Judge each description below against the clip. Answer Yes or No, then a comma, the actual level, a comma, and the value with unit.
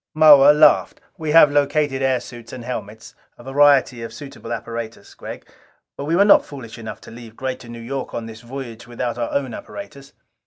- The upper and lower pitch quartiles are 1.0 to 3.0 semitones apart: No, average, 3.4 semitones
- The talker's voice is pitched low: Yes, low, 130 Hz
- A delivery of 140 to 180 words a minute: No, average, 190 wpm